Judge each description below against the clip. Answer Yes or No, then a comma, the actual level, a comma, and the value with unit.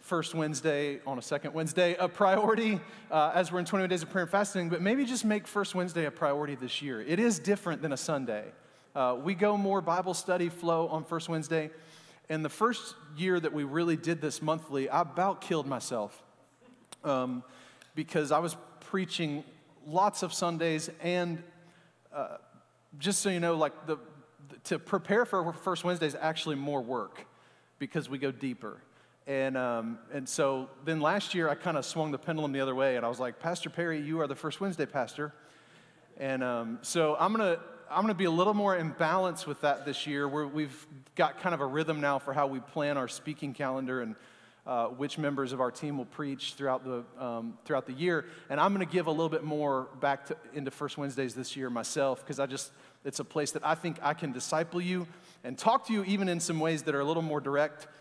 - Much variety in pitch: No, average, 3.8 semitones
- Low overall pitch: No, medium, 155 Hz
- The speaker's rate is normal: No, fast, 215 wpm